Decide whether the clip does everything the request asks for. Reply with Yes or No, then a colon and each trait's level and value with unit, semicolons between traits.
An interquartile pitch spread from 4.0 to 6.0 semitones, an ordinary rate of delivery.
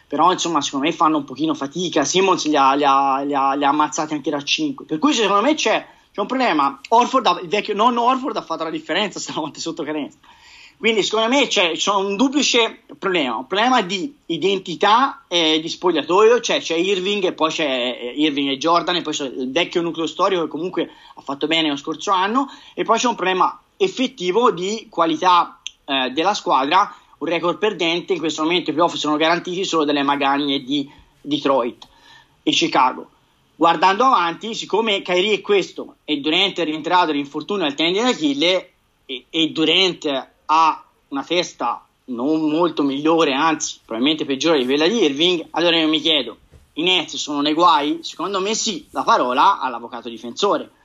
No: average, 5.3 semitones; fast, 185 wpm